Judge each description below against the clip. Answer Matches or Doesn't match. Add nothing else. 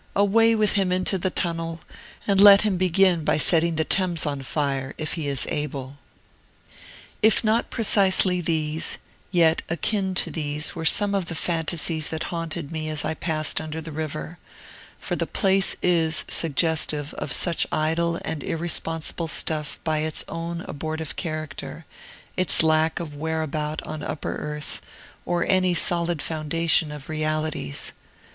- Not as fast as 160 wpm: Matches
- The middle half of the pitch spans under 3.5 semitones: Matches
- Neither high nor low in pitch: Matches